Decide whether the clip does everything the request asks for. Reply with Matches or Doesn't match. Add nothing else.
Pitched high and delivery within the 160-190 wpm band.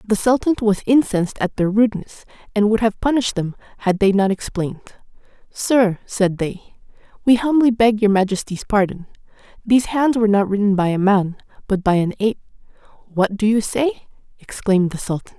Matches